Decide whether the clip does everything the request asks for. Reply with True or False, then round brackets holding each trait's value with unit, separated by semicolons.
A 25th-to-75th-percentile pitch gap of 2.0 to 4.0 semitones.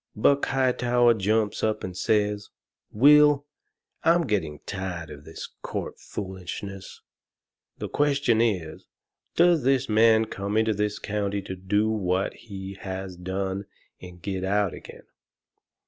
True (3.5 semitones)